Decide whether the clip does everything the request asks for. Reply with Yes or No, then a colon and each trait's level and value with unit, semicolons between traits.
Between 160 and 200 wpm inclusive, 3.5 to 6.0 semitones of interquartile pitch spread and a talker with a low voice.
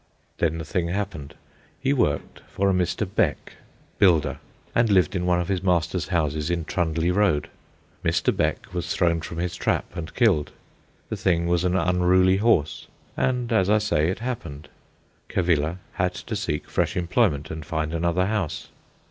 No: average, 165 wpm; average, 2.8 semitones; very low, 90 Hz